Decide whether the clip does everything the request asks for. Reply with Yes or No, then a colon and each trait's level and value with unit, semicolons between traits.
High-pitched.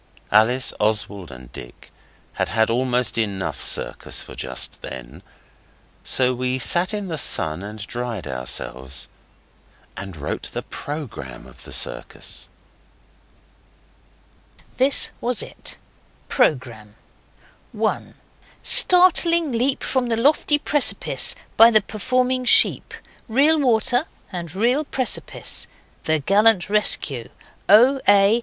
No: medium, 170 Hz